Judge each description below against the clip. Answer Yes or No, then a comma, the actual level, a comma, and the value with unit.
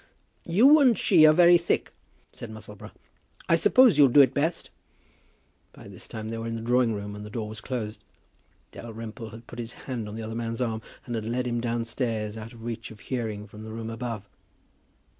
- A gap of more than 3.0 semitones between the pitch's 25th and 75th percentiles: No, narrow, 2.5 semitones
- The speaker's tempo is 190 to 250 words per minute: Yes, fast, 205 wpm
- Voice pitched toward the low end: Yes, low, 115 Hz